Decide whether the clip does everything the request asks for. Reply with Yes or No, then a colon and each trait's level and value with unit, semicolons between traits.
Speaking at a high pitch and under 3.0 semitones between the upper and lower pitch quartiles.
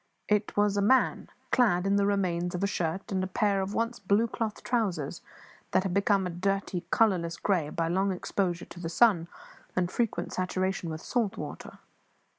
Yes: high, 195 Hz; narrow, 2.6 semitones